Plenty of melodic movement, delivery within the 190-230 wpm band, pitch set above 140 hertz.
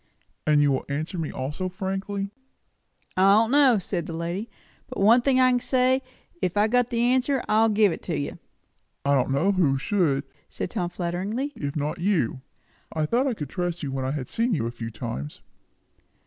Yes: wide, 7.6 semitones; average, 200 wpm; medium, 185 Hz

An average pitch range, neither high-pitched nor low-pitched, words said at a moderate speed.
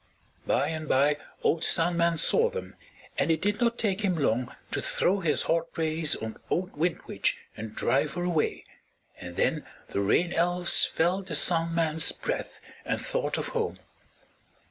Yes: average, 3.2 semitones; medium, 165 Hz; average, 170 wpm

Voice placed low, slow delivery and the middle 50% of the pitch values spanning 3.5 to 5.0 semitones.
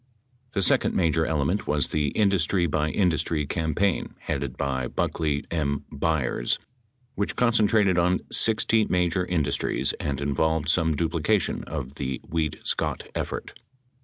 Yes: very low, 80 Hz; slow, 130 wpm; average, 4.1 semitones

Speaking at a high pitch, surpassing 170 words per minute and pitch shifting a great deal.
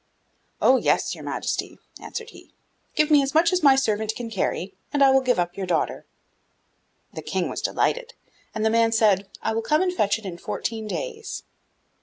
Yes: high, 230 Hz; average, 195 wpm; wide, 6.2 semitones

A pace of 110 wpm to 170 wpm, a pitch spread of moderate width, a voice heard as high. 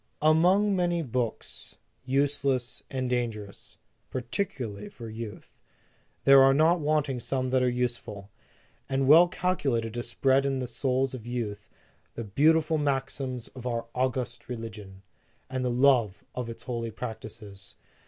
No: average, 145 wpm; average, 3.0 semitones; low, 125 Hz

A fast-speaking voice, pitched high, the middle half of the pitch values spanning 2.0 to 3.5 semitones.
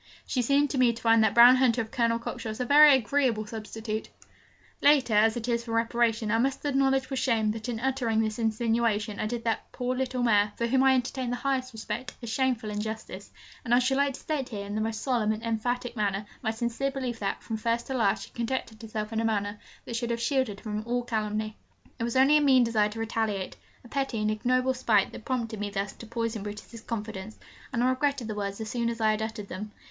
Yes: fast, 235 wpm; high, 230 Hz; average, 2.7 semitones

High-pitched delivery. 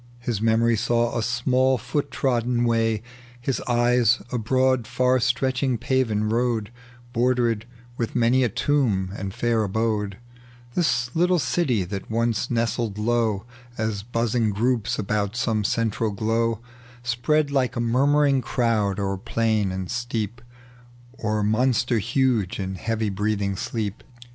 No: low, 115 Hz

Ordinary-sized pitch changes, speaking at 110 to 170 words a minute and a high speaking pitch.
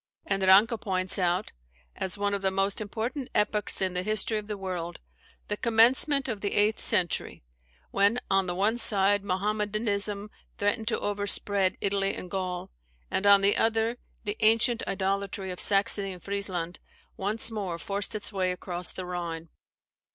No: narrow, 2.1 semitones; average, 165 wpm; high, 200 Hz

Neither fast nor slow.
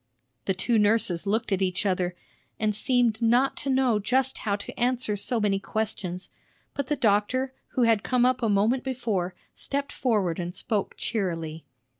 Yes: average, 170 wpm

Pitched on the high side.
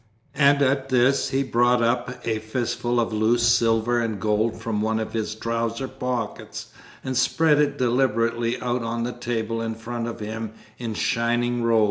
No: low, 120 Hz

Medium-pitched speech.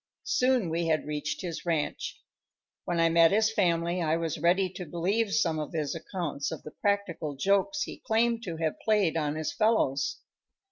Yes: medium, 170 Hz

